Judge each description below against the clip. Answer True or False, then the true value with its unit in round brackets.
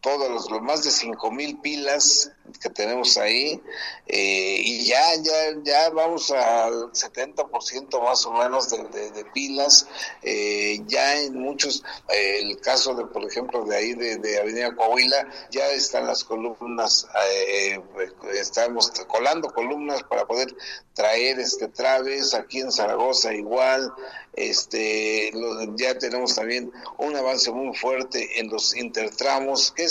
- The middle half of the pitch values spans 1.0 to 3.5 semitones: False (4.1 semitones)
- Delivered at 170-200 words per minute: False (150 wpm)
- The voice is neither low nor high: False (130 Hz)